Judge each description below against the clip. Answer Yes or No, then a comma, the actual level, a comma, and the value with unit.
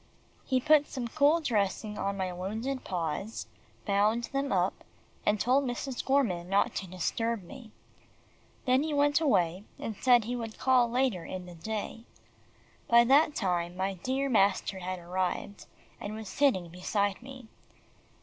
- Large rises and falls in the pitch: Yes, wide, 5.7 semitones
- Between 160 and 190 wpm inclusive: No, average, 150 wpm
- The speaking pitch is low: No, high, 220 Hz